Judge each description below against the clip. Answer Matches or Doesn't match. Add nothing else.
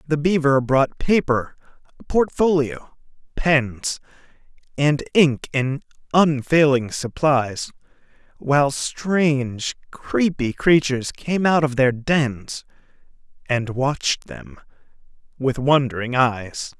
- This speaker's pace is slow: Matches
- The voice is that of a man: Matches